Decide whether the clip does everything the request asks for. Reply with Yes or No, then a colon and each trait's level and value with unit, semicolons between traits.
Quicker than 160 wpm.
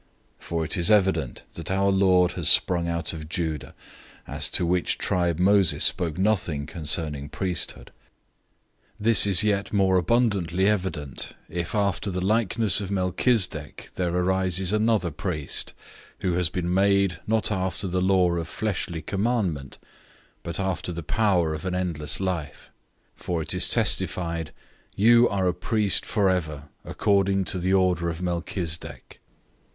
No: average, 150 wpm